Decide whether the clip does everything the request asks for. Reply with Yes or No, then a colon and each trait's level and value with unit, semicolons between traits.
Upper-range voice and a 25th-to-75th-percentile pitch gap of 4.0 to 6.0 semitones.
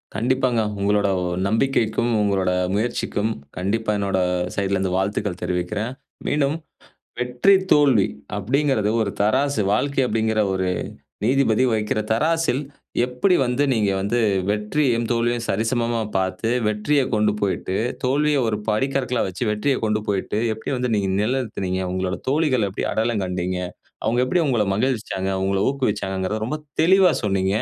No: low, 110 Hz; average, 4.4 semitones